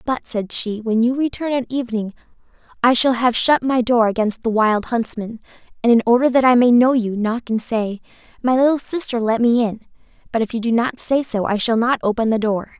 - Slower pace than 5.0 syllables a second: No, 5.5 syllables/s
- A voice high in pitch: Yes, high, 235 Hz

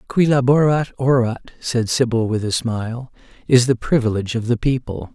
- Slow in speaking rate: No, average, 165 wpm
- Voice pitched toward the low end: Yes, low, 120 Hz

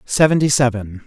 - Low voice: Yes, low, 125 Hz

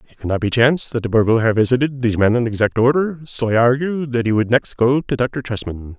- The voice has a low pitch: Yes, low, 120 Hz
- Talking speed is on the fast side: Yes, fast, 260 wpm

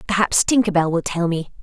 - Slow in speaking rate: No, fast, 220 wpm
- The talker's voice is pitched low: No, medium, 185 Hz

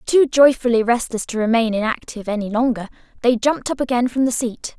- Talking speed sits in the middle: Yes, average, 190 wpm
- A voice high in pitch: Yes, high, 240 Hz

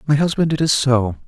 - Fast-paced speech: Yes, fast, 235 wpm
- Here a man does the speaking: Yes, male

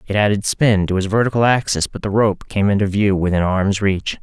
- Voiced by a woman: No, male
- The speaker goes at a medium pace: No, fast, 225 wpm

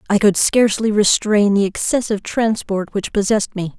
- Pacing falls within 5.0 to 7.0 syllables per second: Yes, 5.3 syllables/s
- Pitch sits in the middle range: No, high, 205 Hz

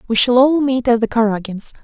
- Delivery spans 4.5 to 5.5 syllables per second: No, 5.8 syllables/s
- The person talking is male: No, female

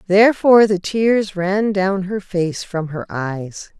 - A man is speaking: No, female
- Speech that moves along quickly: No, average, 160 wpm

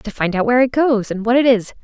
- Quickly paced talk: Yes, fast, 325 wpm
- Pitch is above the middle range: Yes, high, 235 Hz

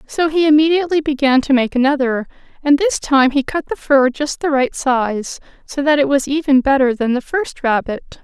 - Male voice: No, female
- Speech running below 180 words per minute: No, fast, 205 wpm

